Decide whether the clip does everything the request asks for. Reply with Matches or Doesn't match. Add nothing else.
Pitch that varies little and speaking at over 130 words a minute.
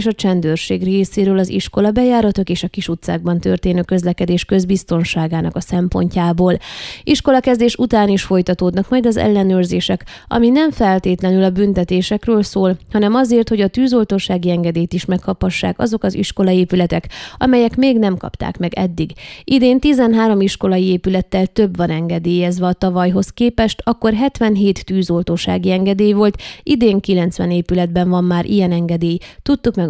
Doesn't match